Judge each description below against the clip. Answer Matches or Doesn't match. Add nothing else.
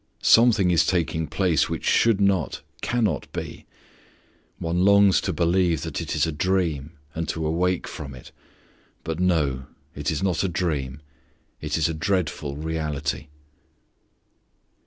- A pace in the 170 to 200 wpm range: Doesn't match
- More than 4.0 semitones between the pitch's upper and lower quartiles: Doesn't match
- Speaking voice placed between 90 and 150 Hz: Doesn't match